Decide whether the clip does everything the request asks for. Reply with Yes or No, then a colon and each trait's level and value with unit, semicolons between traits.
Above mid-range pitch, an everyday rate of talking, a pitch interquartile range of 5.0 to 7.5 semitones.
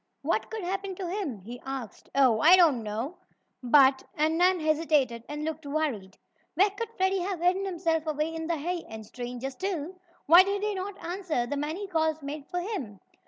Yes: very high, 315 Hz; average, 195 wpm; wide, 5.4 semitones